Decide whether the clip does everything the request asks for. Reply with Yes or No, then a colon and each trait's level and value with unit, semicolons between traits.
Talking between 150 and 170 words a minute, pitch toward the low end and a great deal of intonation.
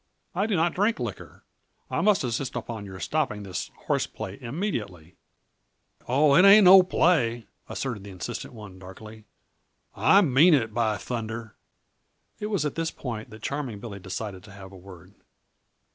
Yes: average, 160 wpm; low, 115 Hz; wide, 7.8 semitones